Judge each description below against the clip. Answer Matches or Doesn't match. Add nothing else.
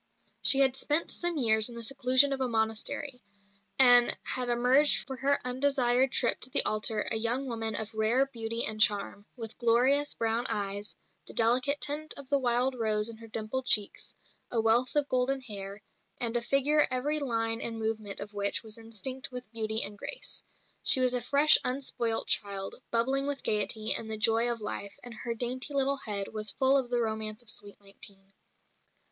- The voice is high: Matches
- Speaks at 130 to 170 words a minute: Doesn't match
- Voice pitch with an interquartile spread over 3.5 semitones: Doesn't match